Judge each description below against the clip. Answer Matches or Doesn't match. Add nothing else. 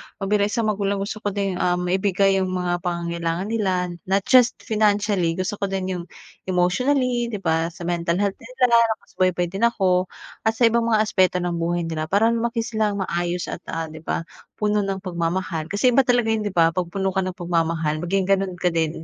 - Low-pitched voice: Doesn't match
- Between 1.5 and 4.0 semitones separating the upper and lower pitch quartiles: Matches